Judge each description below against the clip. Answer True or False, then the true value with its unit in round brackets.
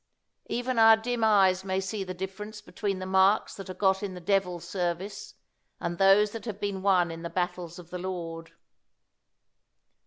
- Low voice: False (190 Hz)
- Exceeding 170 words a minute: True (180 wpm)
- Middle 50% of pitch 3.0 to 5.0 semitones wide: False (2.5 semitones)